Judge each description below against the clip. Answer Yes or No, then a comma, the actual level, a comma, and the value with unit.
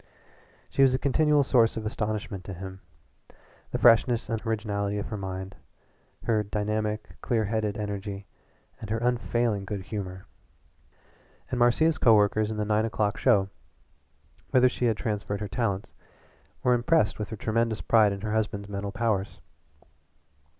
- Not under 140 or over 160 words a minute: Yes, average, 150 wpm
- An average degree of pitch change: No, narrow, 2.3 semitones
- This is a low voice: Yes, low, 110 Hz